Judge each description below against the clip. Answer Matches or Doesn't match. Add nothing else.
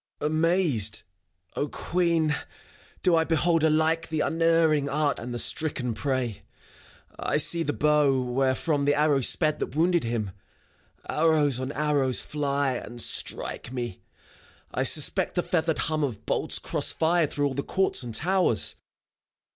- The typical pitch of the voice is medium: Matches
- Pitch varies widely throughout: Doesn't match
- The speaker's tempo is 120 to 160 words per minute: Matches